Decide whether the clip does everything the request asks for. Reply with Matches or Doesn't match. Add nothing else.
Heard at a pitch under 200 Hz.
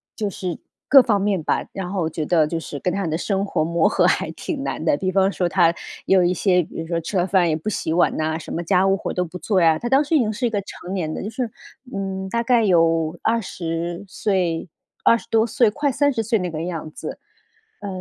Matches